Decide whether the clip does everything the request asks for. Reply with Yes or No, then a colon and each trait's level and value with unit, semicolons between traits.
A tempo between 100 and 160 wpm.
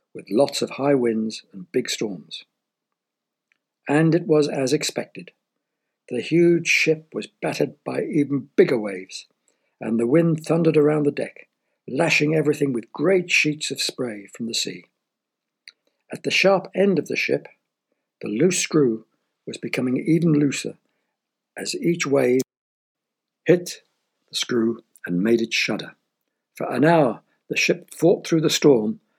Yes: average, 150 wpm